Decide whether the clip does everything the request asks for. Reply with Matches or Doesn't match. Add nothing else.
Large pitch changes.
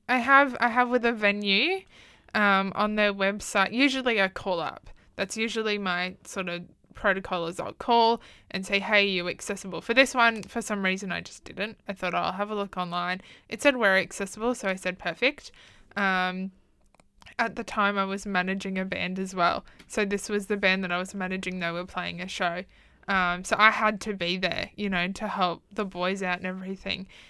Doesn't match